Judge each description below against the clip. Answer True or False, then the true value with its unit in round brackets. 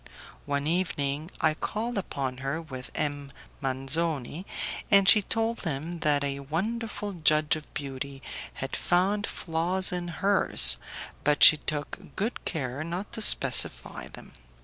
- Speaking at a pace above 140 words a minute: False (135 wpm)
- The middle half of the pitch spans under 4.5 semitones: False (5.0 semitones)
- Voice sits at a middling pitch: True (155 Hz)